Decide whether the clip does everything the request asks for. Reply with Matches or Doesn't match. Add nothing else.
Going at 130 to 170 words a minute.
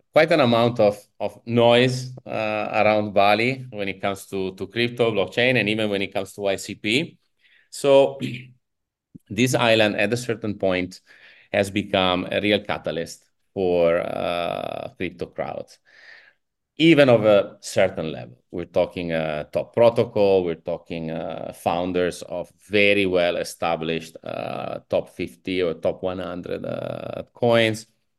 Matches